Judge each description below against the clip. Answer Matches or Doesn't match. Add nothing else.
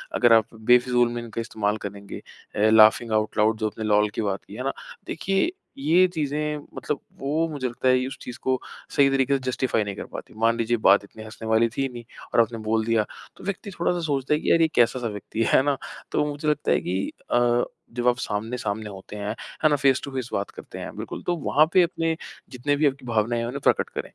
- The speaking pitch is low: Matches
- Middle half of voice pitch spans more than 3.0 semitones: Matches